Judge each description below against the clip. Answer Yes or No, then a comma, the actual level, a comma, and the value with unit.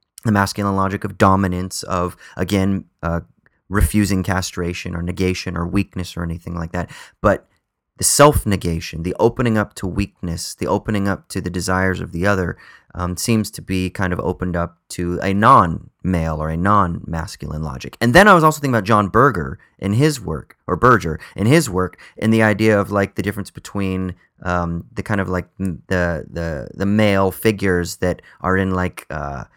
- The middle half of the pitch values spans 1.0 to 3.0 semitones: Yes, narrow, 2.6 semitones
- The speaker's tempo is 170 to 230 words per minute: Yes, average, 180 wpm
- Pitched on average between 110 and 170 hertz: No, very low, 95 Hz